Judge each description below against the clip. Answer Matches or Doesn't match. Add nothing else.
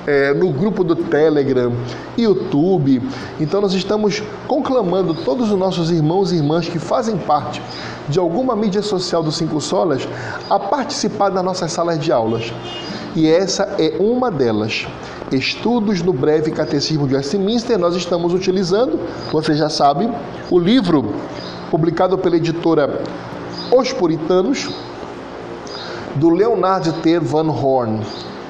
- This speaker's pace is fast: Doesn't match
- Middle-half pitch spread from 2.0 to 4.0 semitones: Doesn't match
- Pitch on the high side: Doesn't match